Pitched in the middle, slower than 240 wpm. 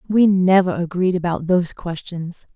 Yes: medium, 180 Hz; average, 140 wpm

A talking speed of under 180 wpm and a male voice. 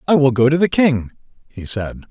No: fast, 230 wpm; male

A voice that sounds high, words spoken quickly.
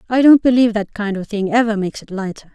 Yes: high, 215 Hz; fast, 260 wpm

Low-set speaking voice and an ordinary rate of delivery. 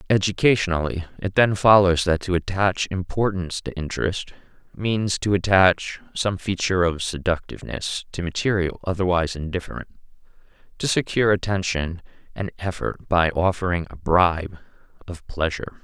No: very low, 90 Hz; slow, 120 wpm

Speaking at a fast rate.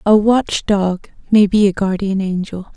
No: average, 175 wpm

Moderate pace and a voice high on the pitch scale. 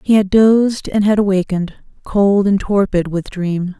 Yes: average, 175 wpm; high, 195 Hz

